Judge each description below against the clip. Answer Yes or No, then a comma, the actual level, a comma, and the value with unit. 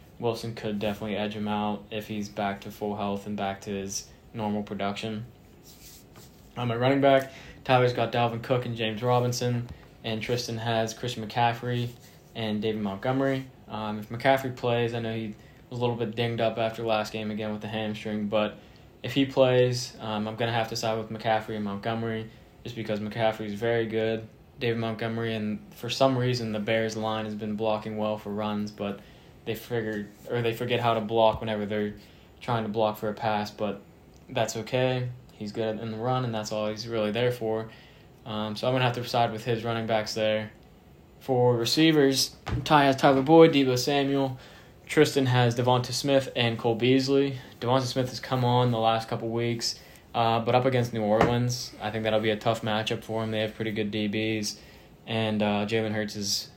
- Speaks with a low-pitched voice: Yes, low, 115 Hz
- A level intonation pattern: Yes, narrow, 2.3 semitones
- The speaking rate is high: No, average, 195 wpm